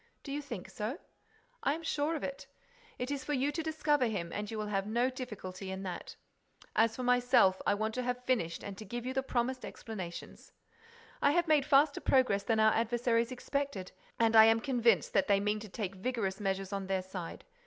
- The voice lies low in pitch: No, high, 230 Hz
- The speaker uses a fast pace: Yes, fast, 210 wpm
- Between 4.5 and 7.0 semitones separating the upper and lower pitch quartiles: Yes, average, 4.8 semitones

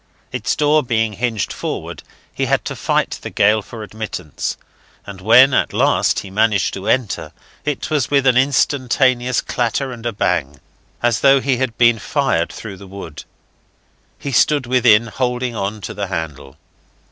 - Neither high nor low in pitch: No, low, 115 Hz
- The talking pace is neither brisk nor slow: Yes, average, 165 wpm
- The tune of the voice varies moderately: Yes, average, 4.4 semitones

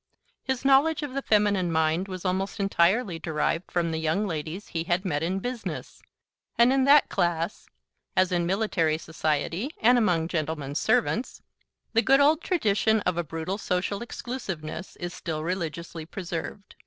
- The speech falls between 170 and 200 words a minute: No, average, 155 wpm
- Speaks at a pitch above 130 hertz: Yes, medium, 185 Hz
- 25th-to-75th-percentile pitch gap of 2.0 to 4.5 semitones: No, average, 5.2 semitones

